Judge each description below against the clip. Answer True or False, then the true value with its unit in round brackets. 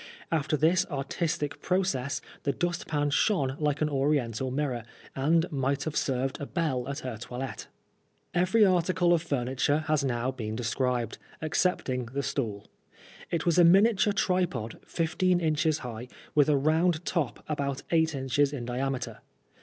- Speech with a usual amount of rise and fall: True (4.3 semitones)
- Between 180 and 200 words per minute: False (150 wpm)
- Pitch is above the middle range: False (145 Hz)